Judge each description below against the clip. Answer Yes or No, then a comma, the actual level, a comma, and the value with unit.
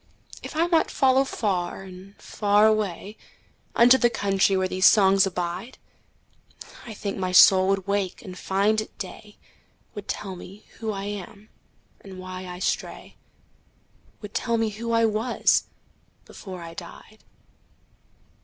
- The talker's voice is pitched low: No, high, 200 Hz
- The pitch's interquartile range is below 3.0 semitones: Yes, narrow, 2.6 semitones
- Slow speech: Yes, slow, 130 wpm